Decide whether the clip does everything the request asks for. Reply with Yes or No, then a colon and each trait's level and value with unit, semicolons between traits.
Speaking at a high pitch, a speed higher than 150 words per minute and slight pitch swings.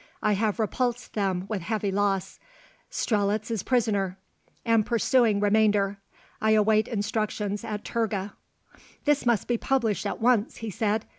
No: high, 215 Hz; average, 140 wpm; narrow, 2.0 semitones